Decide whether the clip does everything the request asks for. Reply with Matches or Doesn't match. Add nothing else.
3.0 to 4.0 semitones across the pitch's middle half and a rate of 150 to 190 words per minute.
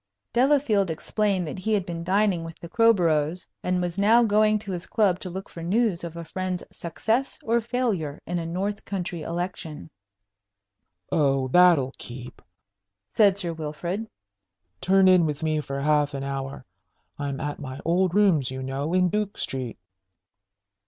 Doesn't match